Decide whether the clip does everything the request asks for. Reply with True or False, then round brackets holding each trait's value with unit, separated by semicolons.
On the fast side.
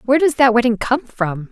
True (235 wpm)